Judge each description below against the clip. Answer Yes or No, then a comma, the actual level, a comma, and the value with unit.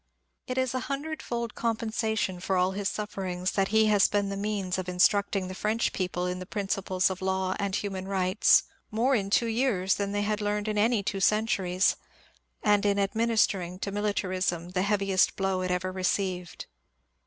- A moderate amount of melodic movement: No, narrow, 2.3 semitones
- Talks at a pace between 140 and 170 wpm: No, average, 185 wpm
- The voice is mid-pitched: No, high, 200 Hz